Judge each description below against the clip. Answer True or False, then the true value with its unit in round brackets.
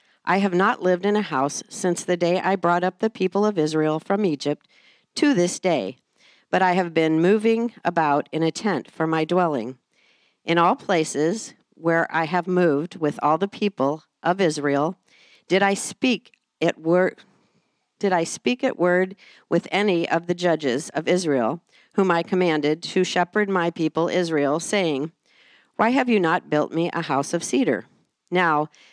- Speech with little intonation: False (3.6 semitones)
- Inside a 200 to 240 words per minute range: False (175 wpm)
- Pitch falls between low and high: True (175 Hz)